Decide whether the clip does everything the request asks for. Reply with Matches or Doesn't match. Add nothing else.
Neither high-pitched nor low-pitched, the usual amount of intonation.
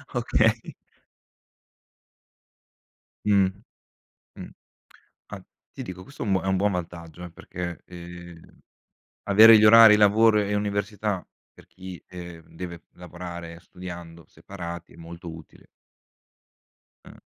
Doesn't match